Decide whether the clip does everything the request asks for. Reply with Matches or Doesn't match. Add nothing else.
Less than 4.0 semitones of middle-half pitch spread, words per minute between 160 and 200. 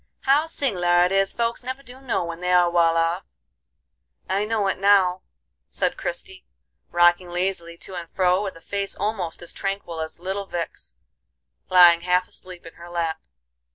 Matches